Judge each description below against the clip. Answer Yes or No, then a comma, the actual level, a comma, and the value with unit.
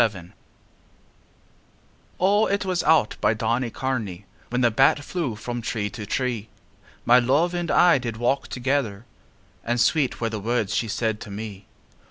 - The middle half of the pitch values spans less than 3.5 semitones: No, average, 4.0 semitones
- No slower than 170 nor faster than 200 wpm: No, average, 155 wpm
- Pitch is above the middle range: No, low, 120 Hz